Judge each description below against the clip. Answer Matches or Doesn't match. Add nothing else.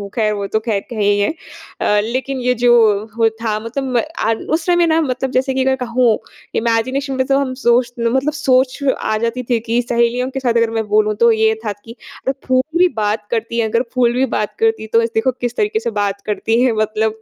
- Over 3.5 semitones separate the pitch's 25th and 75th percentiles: Doesn't match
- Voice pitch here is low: Doesn't match